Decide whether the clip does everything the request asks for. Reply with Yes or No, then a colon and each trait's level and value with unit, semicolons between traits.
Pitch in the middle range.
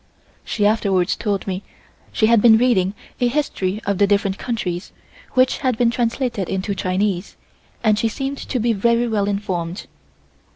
No: high, 210 Hz